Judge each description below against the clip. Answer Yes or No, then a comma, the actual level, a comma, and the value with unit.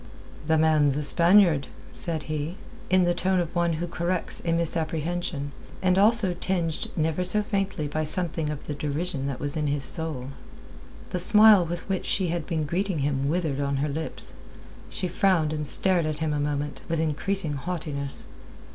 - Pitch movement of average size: Yes, average, 3.3 semitones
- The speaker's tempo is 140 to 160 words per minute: No, average, 175 wpm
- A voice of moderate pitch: Yes, medium, 160 Hz